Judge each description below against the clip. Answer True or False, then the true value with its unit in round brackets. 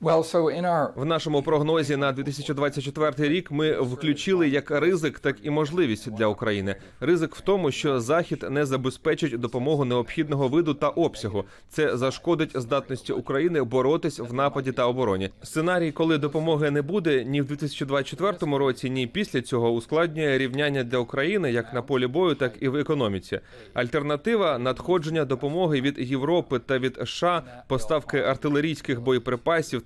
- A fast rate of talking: False (145 wpm)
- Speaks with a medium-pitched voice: True (145 Hz)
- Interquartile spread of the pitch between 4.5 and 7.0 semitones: False (3.5 semitones)